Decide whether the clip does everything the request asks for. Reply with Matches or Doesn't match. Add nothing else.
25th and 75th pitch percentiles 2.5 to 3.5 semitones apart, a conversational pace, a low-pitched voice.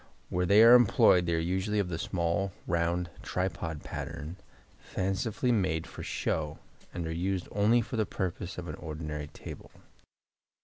Matches